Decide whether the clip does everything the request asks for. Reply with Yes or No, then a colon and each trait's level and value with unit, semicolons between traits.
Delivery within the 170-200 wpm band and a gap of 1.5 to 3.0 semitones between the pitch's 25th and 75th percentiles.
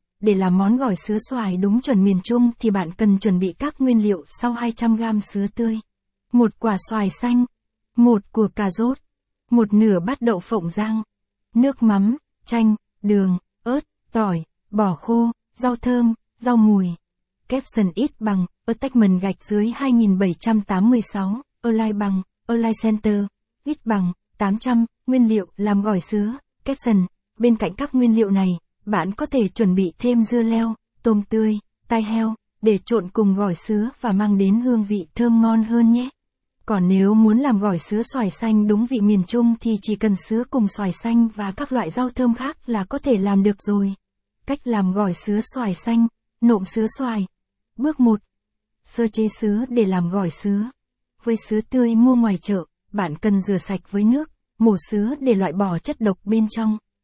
Yes: average, 185 wpm; average, 2.7 semitones